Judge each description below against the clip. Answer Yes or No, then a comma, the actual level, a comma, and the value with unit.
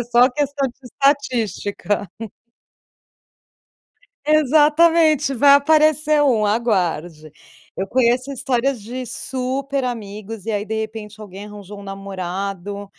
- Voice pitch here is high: Yes, high, 235 Hz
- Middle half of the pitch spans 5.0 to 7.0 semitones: Yes, wide, 5.4 semitones